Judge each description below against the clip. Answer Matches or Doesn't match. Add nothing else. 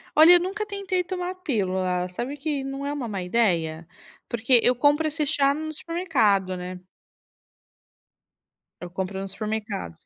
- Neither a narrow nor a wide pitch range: Doesn't match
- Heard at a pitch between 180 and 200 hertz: Doesn't match